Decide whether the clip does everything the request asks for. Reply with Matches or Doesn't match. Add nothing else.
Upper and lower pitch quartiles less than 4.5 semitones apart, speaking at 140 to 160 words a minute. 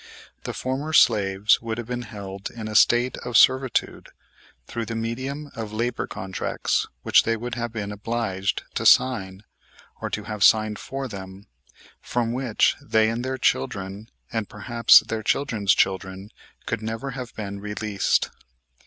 Matches